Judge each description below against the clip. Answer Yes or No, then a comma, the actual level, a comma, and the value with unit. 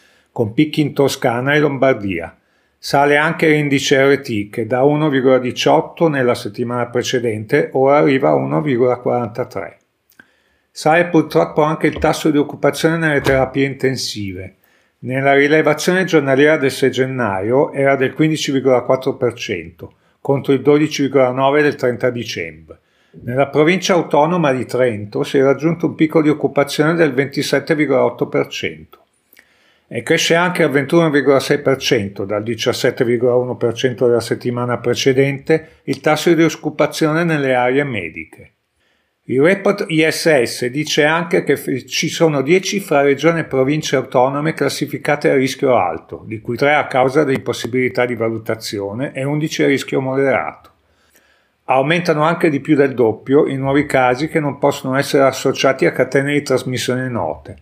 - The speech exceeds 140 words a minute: No, average, 130 wpm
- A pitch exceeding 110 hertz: Yes, medium, 140 Hz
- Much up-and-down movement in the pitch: No, average, 3.4 semitones